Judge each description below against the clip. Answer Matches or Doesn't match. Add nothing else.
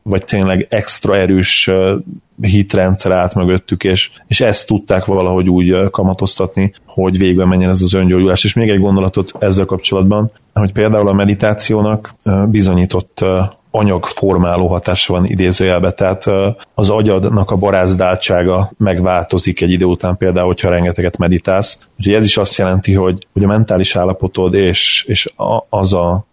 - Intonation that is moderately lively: Doesn't match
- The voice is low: Matches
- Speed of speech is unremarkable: Matches